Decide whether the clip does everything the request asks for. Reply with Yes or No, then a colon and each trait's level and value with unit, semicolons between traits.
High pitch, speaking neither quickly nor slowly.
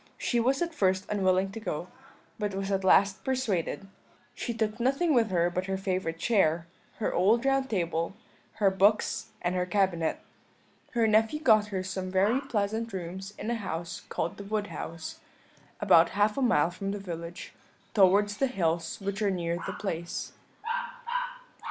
Yes: high, 195 Hz; average, 165 wpm